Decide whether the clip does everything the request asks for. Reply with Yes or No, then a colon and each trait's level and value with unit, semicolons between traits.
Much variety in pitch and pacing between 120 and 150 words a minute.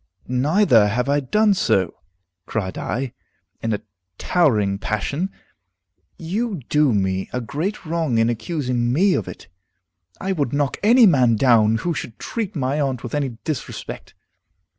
Yes: wide, 6.8 semitones; average, 145 wpm